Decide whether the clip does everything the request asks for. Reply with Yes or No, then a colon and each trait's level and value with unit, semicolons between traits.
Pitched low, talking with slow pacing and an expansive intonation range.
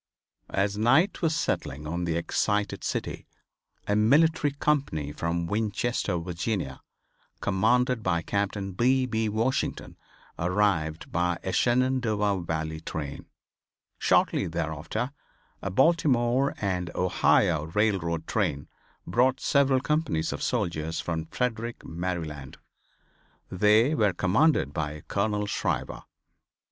Yes: low, 100 Hz; slow, 110 wpm; wide, 6.4 semitones